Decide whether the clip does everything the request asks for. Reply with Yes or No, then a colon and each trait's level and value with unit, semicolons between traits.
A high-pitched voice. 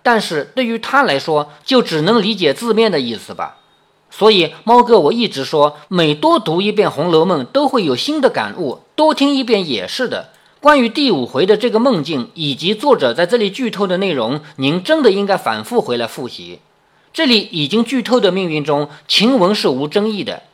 Yes: high, 210 Hz